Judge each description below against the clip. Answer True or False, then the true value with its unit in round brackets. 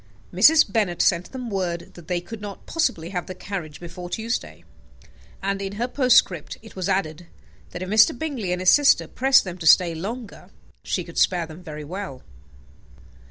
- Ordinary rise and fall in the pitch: True (4.3 semitones)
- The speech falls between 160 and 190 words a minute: True (180 wpm)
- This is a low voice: False (185 Hz)